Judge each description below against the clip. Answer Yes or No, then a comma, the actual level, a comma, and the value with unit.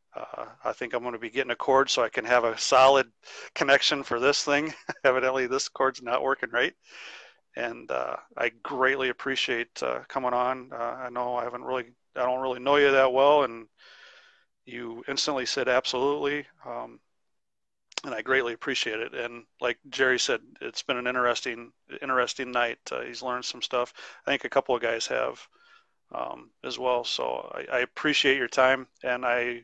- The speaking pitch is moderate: No, low, 125 Hz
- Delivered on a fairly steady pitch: Yes, narrow, 1.5 semitones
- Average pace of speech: Yes, average, 185 wpm